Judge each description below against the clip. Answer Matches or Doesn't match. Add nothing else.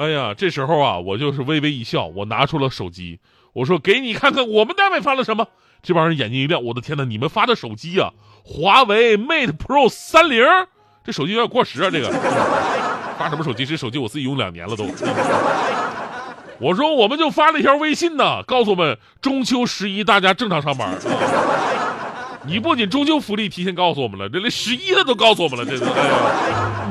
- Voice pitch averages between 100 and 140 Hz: Doesn't match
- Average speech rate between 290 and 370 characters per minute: Matches